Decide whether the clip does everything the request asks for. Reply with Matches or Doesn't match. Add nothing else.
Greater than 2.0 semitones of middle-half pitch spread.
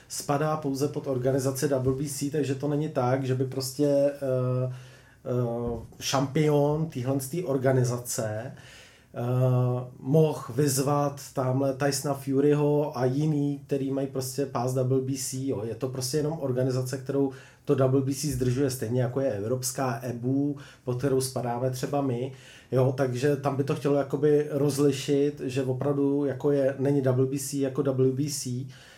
Doesn't match